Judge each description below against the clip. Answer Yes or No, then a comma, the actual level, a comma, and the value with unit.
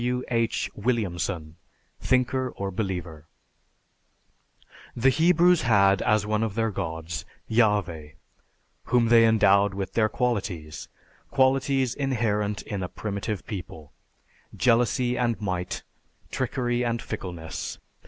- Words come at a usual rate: No, slow, 110 wpm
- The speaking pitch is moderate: No, low, 110 Hz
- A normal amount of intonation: Yes, average, 4.5 semitones